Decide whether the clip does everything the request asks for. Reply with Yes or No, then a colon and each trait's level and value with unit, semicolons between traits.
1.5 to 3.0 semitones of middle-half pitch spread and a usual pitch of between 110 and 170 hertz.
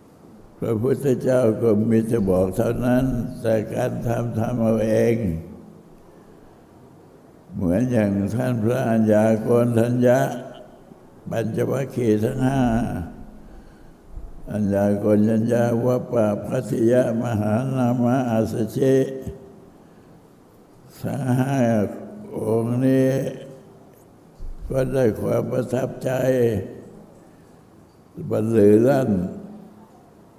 Yes: narrow, 2.5 semitones; low, 120 Hz